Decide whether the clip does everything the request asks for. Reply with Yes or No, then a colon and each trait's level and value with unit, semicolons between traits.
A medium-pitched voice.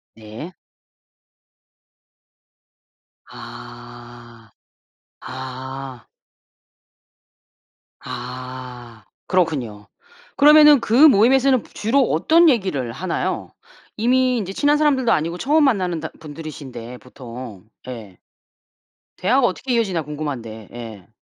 Yes: medium, 155 Hz